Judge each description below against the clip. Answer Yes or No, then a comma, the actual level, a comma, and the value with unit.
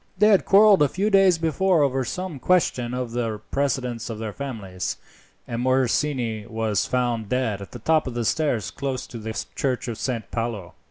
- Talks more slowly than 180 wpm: No, average, 185 wpm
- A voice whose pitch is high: No, low, 125 Hz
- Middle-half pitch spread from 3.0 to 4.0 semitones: No, average, 4.8 semitones